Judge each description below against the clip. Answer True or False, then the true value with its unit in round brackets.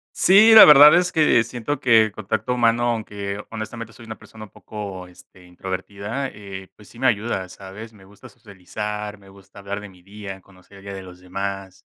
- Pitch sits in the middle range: False (105 Hz)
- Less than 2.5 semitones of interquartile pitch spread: False (2.8 semitones)